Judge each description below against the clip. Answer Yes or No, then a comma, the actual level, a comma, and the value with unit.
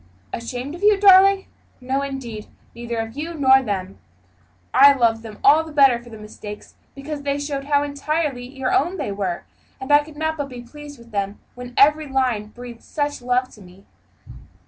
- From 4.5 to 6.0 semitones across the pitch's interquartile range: No, average, 3.9 semitones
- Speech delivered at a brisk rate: No, average, 190 wpm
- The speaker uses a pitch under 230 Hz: No, very high, 265 Hz